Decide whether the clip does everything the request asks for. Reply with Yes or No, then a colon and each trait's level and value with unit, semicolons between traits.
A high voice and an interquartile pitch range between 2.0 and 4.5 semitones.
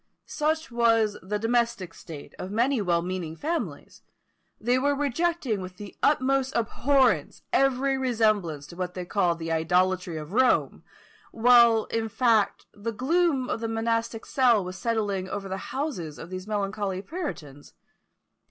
No: high, 220 Hz; wide, 5.6 semitones